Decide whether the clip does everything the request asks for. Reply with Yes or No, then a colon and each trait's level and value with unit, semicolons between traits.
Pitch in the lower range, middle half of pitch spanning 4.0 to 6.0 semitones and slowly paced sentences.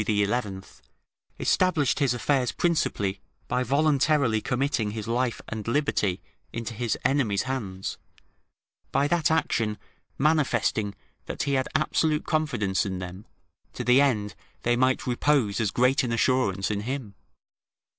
Yes: low, 125 Hz; average, 5.1 semitones; slow, 130 wpm